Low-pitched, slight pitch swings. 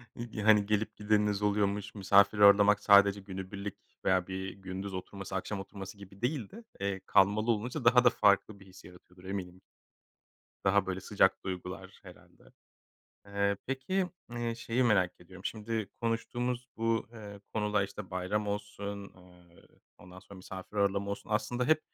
Yes: low, 100 Hz; narrow, 2.1 semitones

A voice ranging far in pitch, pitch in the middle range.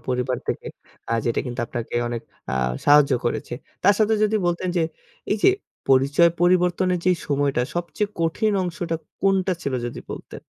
Yes: wide, 5.8 semitones; medium, 170 Hz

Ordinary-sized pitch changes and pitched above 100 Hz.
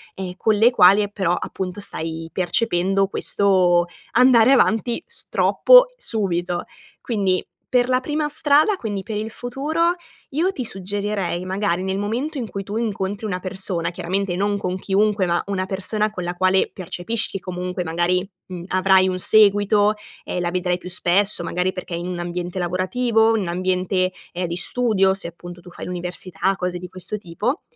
Yes: average, 3.1 semitones; high, 190 Hz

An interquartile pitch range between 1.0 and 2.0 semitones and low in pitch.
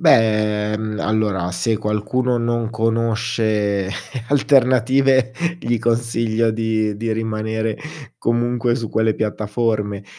Yes: narrow, 1.7 semitones; low, 110 Hz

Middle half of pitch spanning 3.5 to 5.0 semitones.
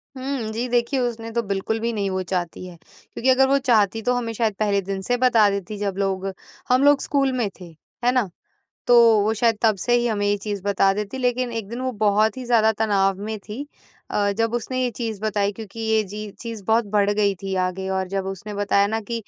No: average, 2.9 semitones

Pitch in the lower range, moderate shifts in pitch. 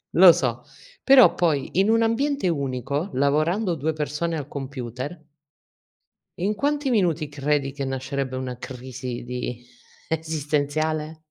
No: medium, 150 Hz; average, 4.3 semitones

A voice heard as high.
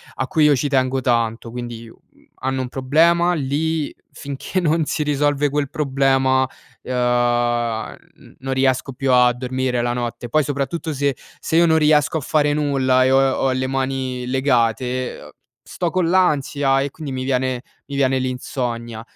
No: low, 135 Hz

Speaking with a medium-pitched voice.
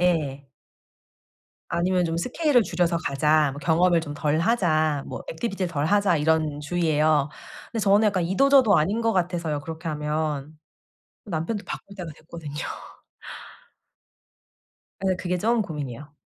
Yes: medium, 165 Hz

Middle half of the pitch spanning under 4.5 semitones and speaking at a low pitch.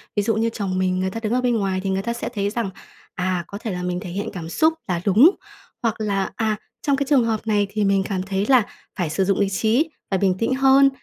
No: average, 3.5 semitones; high, 205 Hz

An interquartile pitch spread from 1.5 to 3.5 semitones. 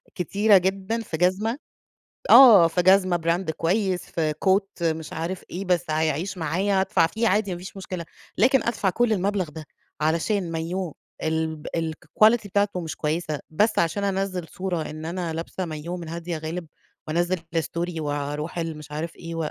Yes: average, 3.1 semitones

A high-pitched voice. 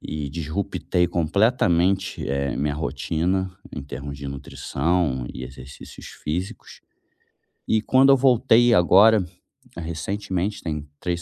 No: very low, 85 Hz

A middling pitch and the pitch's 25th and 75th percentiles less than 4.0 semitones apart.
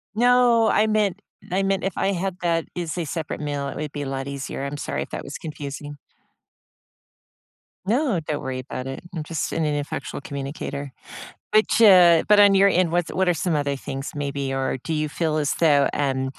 No: medium, 155 Hz; average, 5.1 semitones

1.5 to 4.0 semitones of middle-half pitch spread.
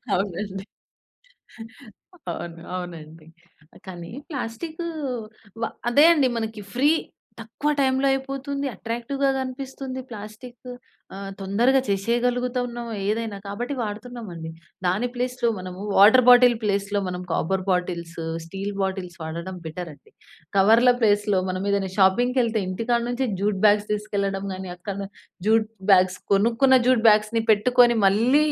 No: average, 4.4 semitones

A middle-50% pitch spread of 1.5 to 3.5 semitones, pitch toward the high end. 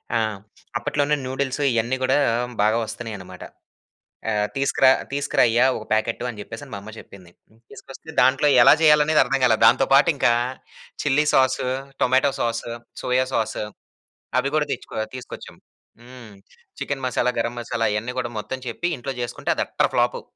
No: average, 3.1 semitones; low, 125 Hz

